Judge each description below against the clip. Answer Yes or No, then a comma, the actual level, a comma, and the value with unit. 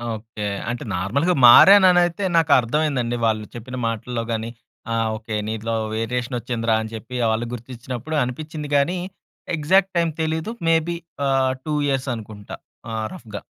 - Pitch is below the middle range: Yes, low, 125 Hz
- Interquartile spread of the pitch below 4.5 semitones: No, wide, 5.6 semitones